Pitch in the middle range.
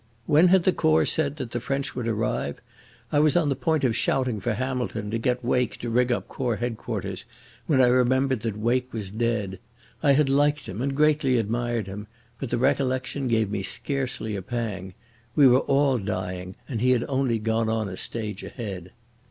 No: low, 120 Hz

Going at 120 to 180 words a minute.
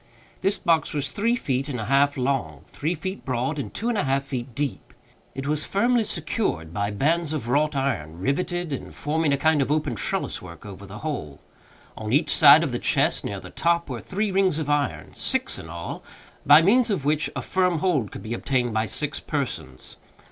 No: average, 200 wpm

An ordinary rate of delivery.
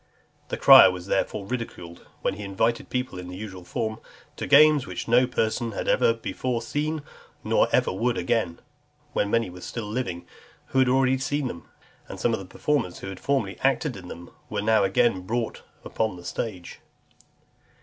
Yes: average, 180 wpm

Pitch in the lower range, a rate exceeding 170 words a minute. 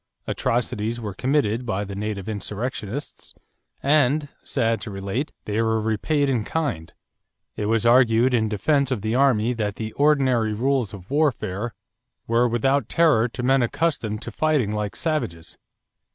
No: low, 115 Hz; average, 150 wpm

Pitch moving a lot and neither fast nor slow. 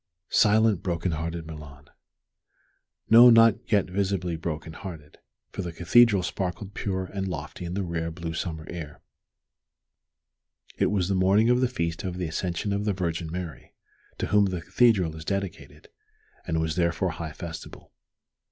No: average, 3.4 semitones; average, 155 wpm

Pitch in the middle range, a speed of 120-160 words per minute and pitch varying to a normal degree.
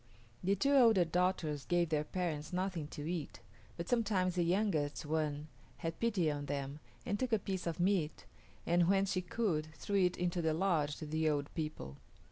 No: medium, 175 Hz; average, 185 wpm; average, 3.8 semitones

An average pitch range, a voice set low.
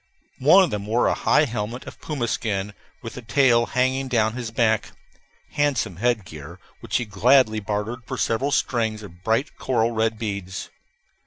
Yes: average, 3.3 semitones; low, 115 Hz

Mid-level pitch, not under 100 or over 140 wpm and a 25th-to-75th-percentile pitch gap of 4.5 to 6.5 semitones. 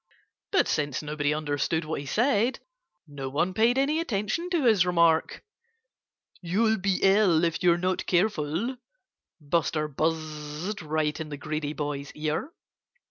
Yes: medium, 165 Hz; slow, 135 wpm; average, 5.3 semitones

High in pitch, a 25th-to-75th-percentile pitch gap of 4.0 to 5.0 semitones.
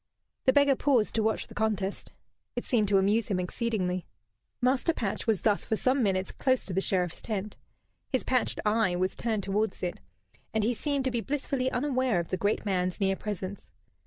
Yes: high, 215 Hz; average, 4.7 semitones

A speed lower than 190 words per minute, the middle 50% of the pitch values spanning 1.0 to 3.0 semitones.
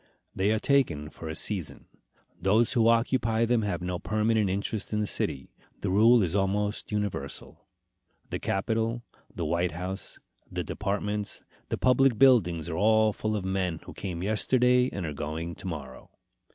No: average, 165 wpm; average, 4.0 semitones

